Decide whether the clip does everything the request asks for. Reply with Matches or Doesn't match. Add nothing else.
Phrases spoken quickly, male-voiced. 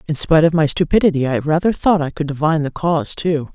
Doesn't match